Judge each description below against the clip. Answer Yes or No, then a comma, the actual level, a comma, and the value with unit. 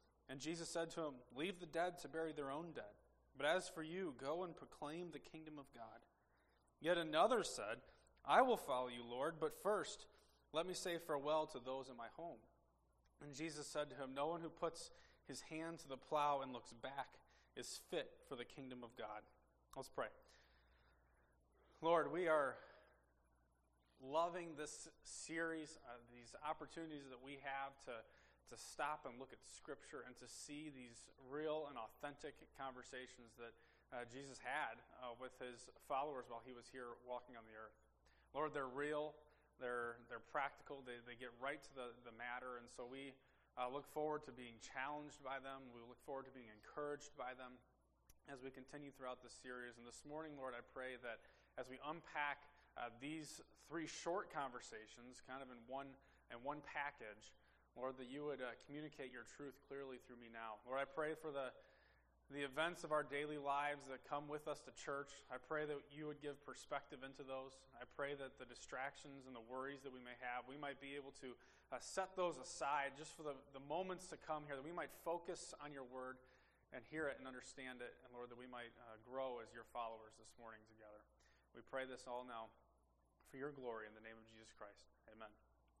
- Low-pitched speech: Yes, low, 130 Hz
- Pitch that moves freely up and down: No, average, 3.6 semitones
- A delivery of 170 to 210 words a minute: Yes, average, 195 wpm